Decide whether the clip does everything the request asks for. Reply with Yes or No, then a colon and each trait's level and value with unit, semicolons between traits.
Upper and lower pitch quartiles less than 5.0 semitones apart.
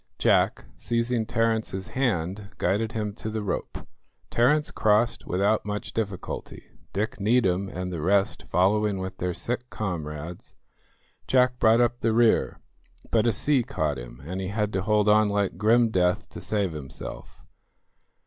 Yes: average, 3.6 semitones